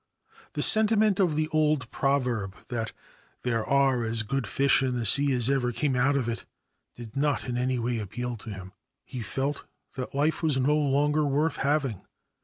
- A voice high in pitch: No, low, 135 Hz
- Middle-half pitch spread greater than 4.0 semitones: No, average, 3.5 semitones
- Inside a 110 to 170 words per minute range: No, average, 195 wpm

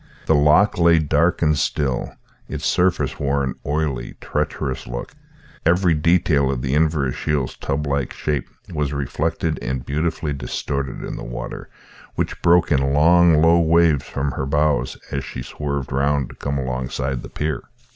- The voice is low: Yes, very low, 70 Hz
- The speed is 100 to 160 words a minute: Yes, average, 155 wpm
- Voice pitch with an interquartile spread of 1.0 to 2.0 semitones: No, average, 2.7 semitones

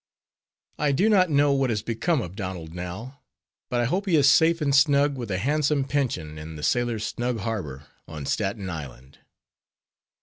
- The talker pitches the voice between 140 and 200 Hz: No, low, 120 Hz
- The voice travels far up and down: Yes, wide, 8.0 semitones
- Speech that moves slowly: No, average, 175 wpm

